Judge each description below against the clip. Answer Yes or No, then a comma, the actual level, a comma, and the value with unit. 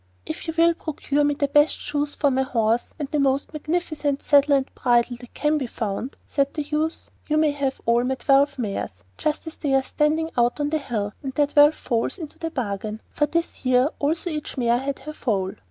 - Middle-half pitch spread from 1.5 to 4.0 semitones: Yes, average, 3.5 semitones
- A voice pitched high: Yes, very high, 285 Hz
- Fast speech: Yes, fast, 220 wpm